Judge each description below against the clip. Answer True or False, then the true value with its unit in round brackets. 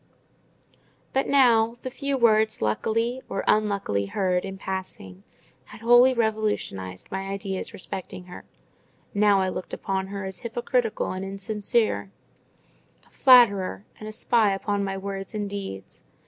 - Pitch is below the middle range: False (200 Hz)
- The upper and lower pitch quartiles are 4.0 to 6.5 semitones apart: False (3.0 semitones)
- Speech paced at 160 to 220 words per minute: False (135 wpm)